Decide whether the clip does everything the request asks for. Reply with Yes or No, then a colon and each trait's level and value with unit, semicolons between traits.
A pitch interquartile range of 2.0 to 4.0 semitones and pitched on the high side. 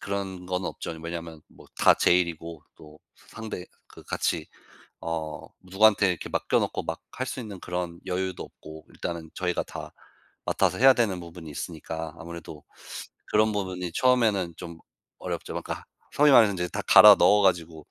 No: average, 3.2 semitones; very low, 90 Hz